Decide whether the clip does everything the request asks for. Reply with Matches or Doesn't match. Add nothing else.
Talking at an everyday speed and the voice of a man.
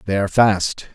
Matches